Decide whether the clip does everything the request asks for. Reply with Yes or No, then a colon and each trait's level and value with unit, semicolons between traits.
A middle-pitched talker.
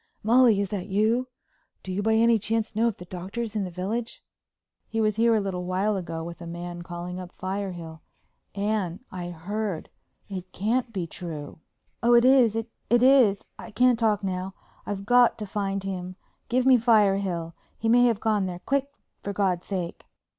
No: high, 200 Hz